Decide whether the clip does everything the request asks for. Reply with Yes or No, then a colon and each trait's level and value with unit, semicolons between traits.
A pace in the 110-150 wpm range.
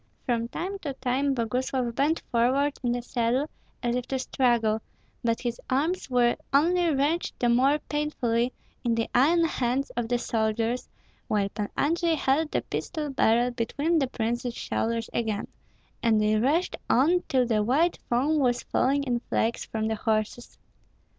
No: average, 160 wpm